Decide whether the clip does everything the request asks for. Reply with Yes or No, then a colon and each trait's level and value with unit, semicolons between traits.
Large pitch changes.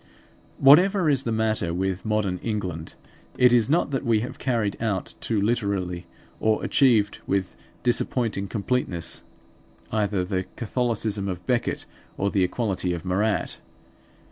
No: average, 4.0 semitones